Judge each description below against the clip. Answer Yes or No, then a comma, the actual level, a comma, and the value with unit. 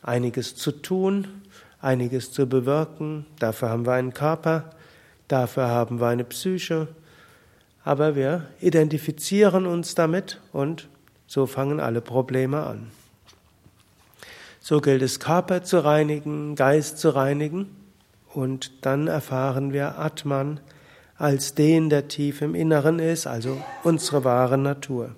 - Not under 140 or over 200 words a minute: No, slow, 125 wpm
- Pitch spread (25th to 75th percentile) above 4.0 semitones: No, average, 3.4 semitones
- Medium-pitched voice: Yes, medium, 145 Hz